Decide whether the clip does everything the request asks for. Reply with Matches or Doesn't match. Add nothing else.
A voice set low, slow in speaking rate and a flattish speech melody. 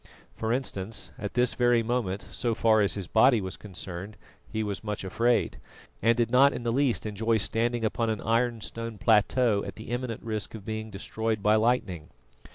Doesn't match